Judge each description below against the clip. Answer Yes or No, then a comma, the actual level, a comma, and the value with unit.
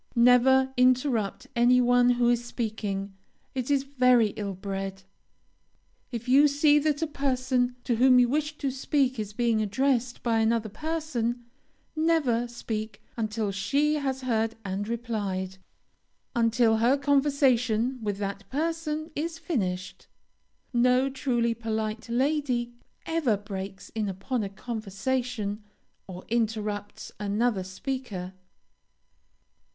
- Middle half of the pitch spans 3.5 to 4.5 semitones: Yes, average, 3.8 semitones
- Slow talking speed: Yes, slow, 120 wpm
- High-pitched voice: Yes, high, 240 Hz